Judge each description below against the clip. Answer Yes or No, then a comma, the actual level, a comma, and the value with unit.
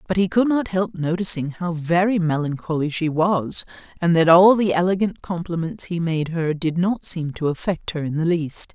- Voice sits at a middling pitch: Yes, medium, 170 Hz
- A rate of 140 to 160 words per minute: No, average, 200 wpm